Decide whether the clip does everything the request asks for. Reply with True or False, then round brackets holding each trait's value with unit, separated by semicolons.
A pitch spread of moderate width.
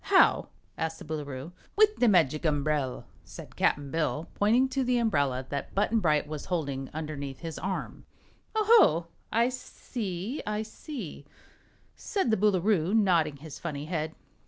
False (6.7 semitones)